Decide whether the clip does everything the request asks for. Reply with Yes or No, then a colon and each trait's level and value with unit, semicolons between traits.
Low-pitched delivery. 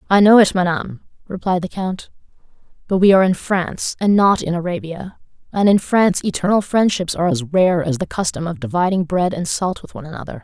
No: medium, 180 Hz